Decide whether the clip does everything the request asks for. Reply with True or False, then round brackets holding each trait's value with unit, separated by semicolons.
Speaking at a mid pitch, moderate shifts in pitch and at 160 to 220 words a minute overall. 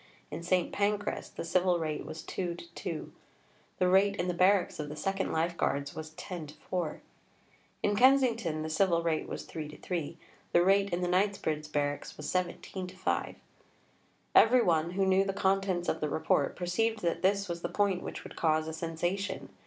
True (180 Hz; 3.4 semitones; 170 wpm)